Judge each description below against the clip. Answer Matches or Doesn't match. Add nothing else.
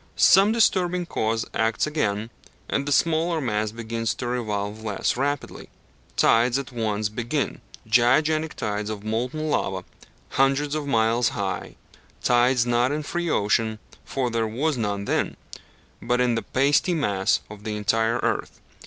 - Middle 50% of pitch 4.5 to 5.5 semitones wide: Matches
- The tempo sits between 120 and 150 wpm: Matches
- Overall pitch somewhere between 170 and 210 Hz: Doesn't match